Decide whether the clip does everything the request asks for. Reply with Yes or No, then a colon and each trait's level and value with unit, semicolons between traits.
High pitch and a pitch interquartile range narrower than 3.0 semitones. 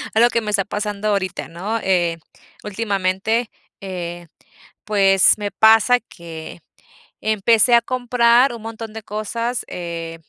No: high, 210 Hz; average, 3.5 semitones